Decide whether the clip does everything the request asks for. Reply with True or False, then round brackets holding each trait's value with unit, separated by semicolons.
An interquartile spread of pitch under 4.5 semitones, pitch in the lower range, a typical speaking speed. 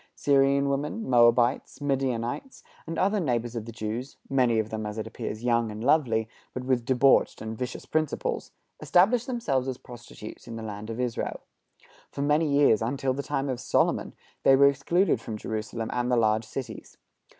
True (3.6 semitones; 125 Hz; 175 wpm)